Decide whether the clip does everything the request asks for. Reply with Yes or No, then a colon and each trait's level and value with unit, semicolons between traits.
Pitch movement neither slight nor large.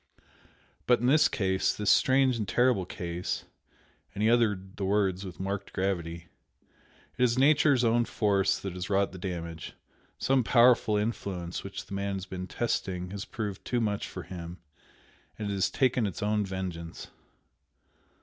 Yes: average, 4.0 semitones